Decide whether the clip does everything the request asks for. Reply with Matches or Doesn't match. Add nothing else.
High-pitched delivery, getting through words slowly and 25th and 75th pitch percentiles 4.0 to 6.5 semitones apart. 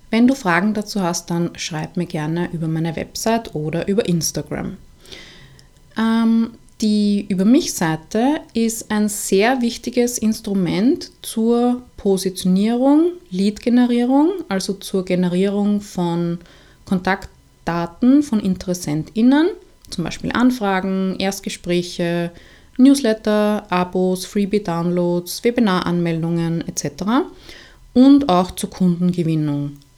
Matches